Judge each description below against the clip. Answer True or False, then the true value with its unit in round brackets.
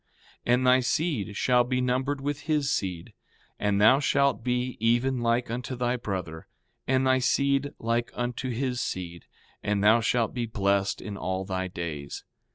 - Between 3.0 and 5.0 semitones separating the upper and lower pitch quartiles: True (4.3 semitones)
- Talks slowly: False (165 wpm)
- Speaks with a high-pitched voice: False (120 Hz)